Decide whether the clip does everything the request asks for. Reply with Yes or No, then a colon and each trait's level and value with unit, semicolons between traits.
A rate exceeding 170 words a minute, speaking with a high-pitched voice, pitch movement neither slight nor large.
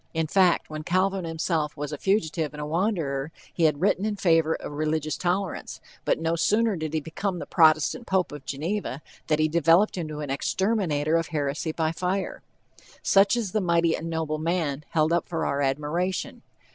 No: average, 185 wpm; medium, 165 Hz; average, 3.2 semitones